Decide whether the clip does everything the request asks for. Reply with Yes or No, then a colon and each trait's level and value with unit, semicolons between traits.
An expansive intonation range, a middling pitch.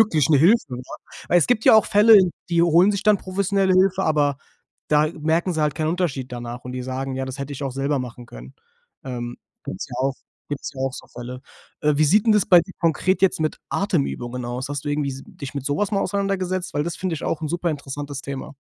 Yes: wide, 5.7 semitones; medium, 150 Hz